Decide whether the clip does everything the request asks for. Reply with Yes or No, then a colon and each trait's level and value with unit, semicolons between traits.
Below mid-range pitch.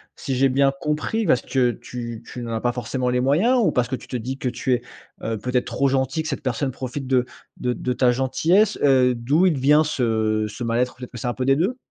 Yes: low, 130 Hz